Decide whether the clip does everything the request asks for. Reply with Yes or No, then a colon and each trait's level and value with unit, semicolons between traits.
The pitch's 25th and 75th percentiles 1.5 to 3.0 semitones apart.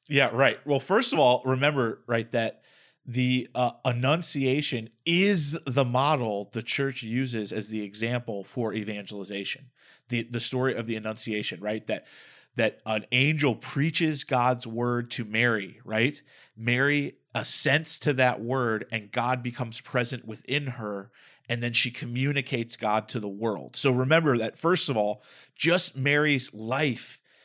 No: average, 3.6 semitones